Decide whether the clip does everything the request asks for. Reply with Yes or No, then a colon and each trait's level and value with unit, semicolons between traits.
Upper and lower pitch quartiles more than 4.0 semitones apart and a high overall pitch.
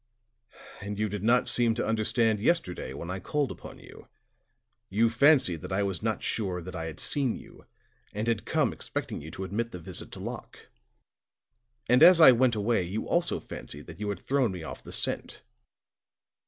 No: average, 4.5 semitones; low, 105 Hz